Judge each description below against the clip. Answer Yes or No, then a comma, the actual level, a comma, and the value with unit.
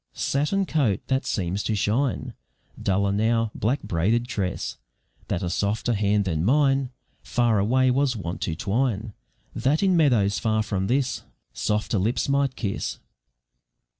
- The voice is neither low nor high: No, low, 110 Hz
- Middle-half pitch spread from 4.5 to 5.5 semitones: Yes, average, 4.8 semitones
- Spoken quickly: No, average, 140 wpm